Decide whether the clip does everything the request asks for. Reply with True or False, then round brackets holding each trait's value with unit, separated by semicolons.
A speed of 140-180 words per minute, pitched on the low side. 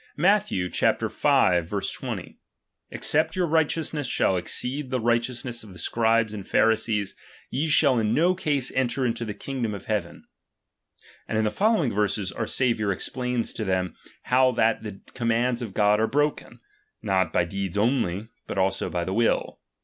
True (160 wpm; 115 Hz)